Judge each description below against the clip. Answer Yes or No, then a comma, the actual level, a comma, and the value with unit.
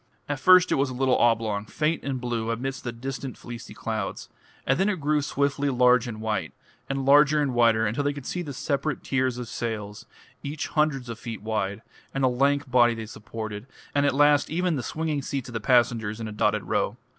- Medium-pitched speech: No, low, 125 Hz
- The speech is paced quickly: Yes, fast, 215 wpm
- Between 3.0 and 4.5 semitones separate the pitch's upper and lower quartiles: Yes, average, 3.9 semitones